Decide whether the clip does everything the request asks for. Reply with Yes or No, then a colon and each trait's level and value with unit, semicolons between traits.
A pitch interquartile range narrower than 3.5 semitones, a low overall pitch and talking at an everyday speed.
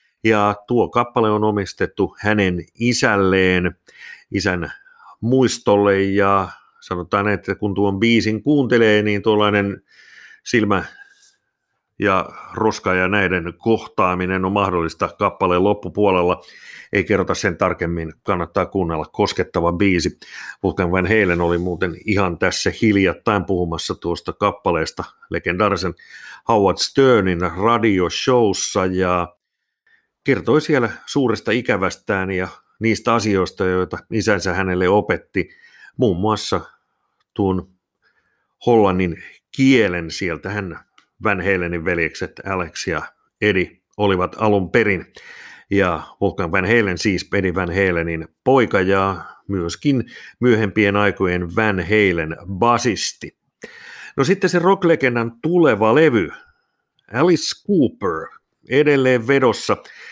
No: average, 3.8 semitones; low, 100 Hz; average, 105 wpm